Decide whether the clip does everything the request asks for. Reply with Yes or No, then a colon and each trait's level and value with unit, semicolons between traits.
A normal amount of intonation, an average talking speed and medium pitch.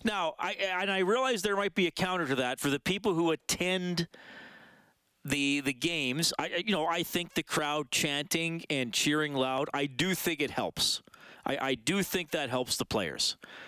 Yes: average, 4.7 semitones; average, 195 wpm; medium, 165 Hz